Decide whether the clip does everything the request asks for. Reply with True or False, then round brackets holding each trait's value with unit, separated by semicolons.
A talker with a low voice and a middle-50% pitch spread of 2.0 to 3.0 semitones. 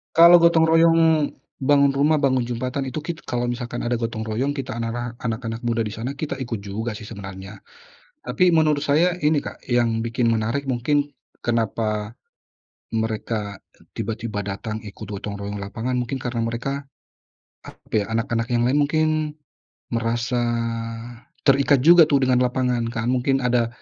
False (120 Hz; 3.8 semitones)